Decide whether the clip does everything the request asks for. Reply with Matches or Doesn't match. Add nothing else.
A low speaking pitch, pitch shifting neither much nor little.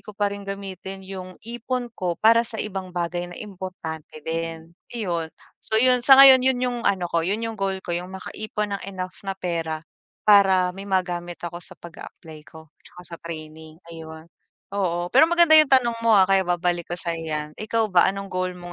Doesn't match